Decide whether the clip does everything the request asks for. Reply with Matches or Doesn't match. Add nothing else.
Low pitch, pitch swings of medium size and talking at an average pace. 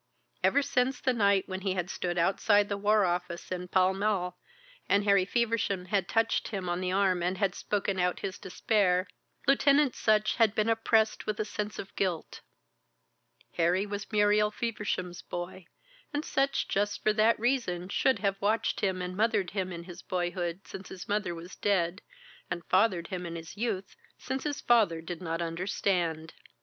Doesn't match